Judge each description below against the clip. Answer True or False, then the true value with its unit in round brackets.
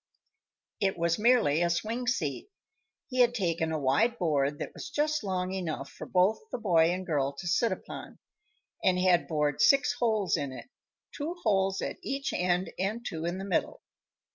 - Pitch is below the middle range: False (185 Hz)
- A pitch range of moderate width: False (6.0 semitones)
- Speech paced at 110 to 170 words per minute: False (180 wpm)